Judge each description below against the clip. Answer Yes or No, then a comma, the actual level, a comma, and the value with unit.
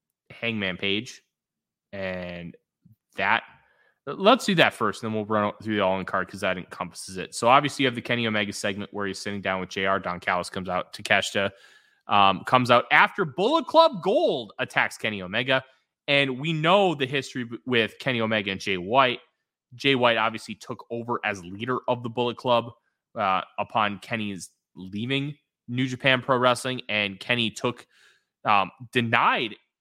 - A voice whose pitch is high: No, low, 115 Hz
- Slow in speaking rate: No, average, 170 wpm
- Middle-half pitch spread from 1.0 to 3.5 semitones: No, average, 4.2 semitones